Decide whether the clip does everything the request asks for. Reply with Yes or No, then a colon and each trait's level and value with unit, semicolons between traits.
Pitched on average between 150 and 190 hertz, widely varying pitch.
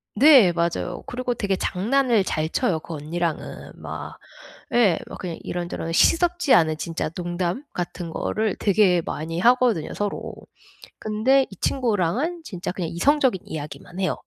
Yes: medium, 185 Hz; wide, 6.2 semitones